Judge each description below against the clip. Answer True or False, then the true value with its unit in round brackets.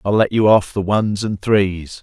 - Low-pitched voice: True (100 Hz)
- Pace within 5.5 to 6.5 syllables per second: False (4.2 syllables/s)